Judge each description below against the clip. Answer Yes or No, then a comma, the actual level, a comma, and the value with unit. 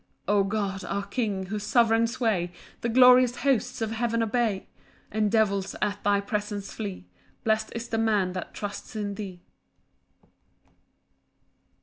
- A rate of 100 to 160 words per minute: Yes, average, 140 wpm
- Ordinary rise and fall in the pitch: No, narrow, 2.3 semitones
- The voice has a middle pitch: No, high, 210 Hz